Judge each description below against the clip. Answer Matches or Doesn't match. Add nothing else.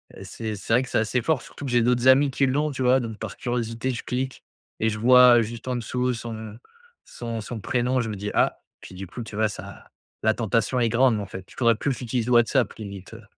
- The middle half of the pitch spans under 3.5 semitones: Matches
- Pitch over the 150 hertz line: Doesn't match